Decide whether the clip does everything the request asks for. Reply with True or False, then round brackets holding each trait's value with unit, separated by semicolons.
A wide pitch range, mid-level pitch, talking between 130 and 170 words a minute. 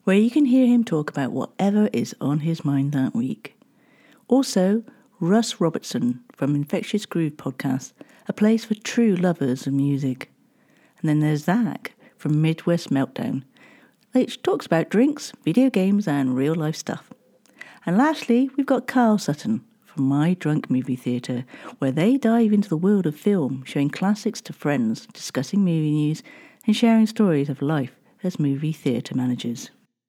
True (7.9 semitones; 180 Hz; 160 wpm)